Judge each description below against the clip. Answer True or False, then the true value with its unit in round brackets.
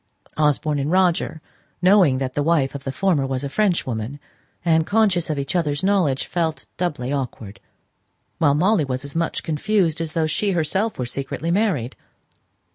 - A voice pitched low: False (155 Hz)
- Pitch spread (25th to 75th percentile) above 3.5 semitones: True (4.5 semitones)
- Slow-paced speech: False (165 wpm)